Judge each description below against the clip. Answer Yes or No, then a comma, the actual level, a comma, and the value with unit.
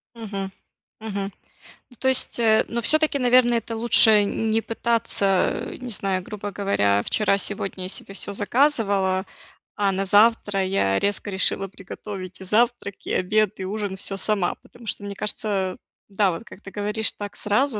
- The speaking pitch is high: Yes, high, 205 Hz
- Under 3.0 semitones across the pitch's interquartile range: Yes, narrow, 2.5 semitones